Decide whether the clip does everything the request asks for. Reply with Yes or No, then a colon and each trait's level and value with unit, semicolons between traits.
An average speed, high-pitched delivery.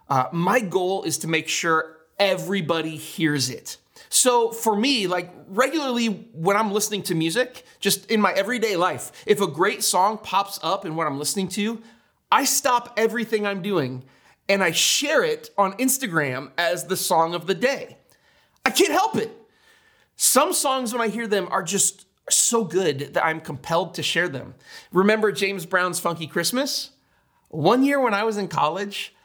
Yes: average, 175 wpm; high, 195 Hz